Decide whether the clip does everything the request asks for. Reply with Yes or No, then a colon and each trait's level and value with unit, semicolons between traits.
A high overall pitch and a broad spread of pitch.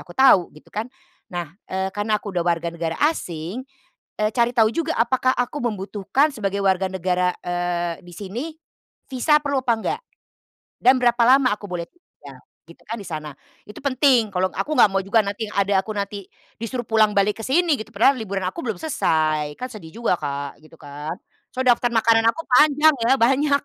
Yes: high, 215 Hz; wide, 5.8 semitones